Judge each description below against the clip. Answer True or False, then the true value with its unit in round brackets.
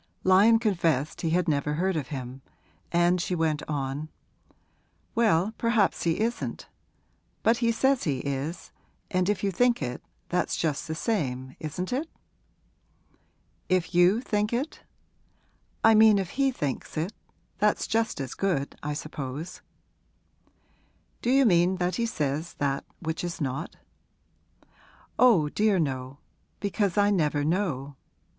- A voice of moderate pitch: True (175 Hz)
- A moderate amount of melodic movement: False (6.1 semitones)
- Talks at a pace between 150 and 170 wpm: False (135 wpm)